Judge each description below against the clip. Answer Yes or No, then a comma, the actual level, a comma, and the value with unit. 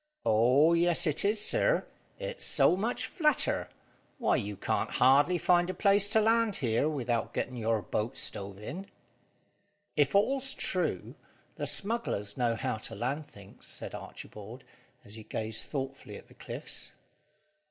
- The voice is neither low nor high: Yes, medium, 145 Hz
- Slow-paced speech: No, average, 150 wpm